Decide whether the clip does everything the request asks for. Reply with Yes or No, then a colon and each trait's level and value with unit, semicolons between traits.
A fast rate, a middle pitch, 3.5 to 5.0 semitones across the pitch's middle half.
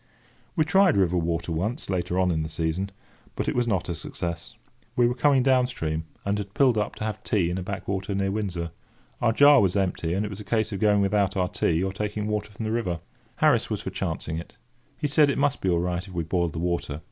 No: fast, 245 wpm; very low, 95 Hz; average, 3.9 semitones